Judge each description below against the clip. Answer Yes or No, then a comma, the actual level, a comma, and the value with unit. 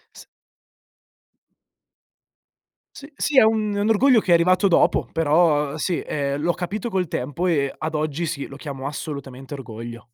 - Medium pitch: Yes, medium, 155 Hz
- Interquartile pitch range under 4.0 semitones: No, average, 5.1 semitones